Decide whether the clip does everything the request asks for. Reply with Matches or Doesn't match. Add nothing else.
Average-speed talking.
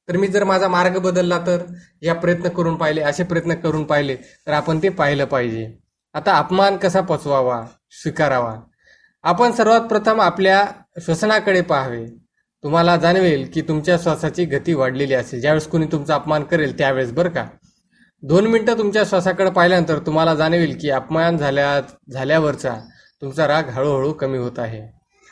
Doesn't match